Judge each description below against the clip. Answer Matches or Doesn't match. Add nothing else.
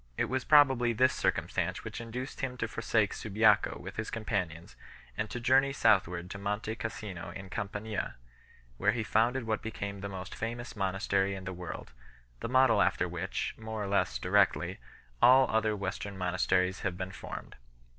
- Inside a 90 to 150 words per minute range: Doesn't match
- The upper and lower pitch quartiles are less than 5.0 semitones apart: Matches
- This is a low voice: Matches